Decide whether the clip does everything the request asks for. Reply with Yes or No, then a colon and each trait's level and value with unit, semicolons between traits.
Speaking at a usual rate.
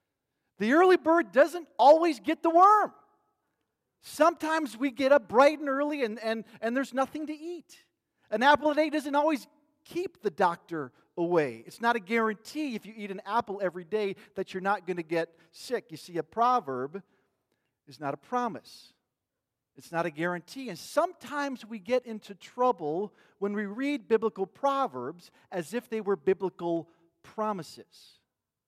Yes: average, 165 wpm